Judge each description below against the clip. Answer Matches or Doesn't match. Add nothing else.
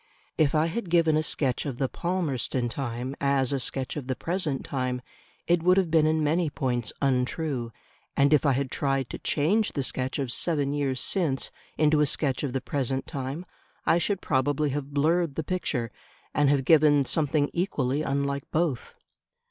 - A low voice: Doesn't match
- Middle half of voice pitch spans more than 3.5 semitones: Doesn't match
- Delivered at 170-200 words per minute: Matches